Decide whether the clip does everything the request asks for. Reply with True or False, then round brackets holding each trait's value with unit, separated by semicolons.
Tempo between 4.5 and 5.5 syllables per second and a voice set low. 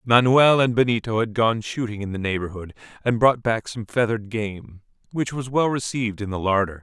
True (5.4 syllables/s; 115 Hz)